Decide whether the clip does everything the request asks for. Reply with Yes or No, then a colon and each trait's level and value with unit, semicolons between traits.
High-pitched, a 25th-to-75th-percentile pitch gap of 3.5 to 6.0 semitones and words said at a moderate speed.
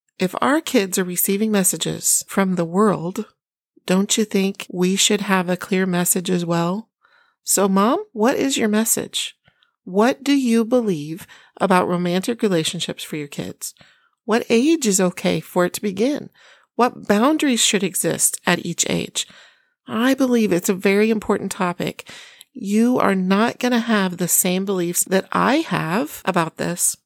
Yes: high, 200 Hz; average, 4.2 semitones; average, 160 wpm